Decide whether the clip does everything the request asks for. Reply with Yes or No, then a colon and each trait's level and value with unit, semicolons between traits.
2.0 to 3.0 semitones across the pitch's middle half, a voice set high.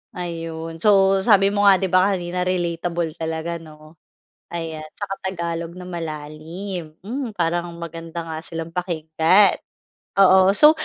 No: narrow, 2.6 semitones; medium, 170 Hz